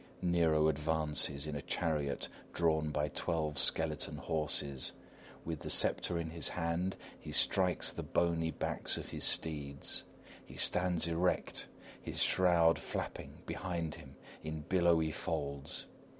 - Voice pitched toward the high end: No, very low, 80 Hz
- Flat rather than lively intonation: Yes, narrow, 2.1 semitones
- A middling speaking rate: No, slow, 130 wpm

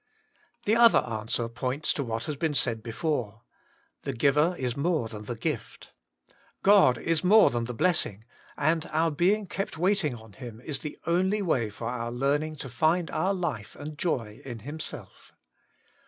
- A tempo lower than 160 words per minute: No, average, 170 wpm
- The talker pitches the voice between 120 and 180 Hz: Yes, medium, 140 Hz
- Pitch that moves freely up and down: Yes, wide, 6.2 semitones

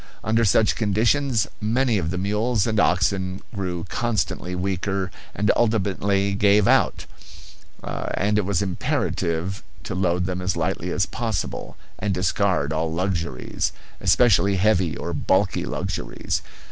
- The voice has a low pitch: Yes, very low, 95 Hz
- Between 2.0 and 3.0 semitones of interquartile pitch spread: Yes, average, 2.7 semitones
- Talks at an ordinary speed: No, slow, 130 wpm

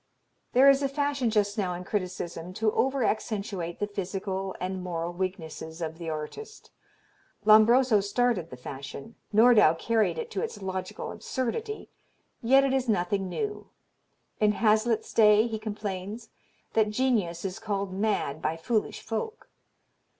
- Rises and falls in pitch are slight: No, average, 4.5 semitones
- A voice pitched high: Yes, high, 210 Hz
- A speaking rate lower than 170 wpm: Yes, average, 145 wpm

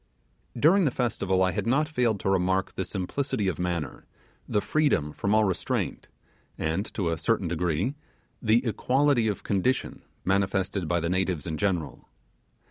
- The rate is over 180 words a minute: No, average, 150 wpm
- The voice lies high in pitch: No, very low, 95 Hz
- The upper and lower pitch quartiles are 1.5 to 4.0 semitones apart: No, average, 4.7 semitones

